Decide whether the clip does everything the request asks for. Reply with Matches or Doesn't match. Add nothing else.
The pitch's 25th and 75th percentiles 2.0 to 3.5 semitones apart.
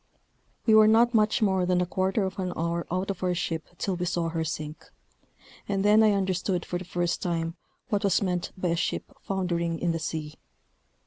Matches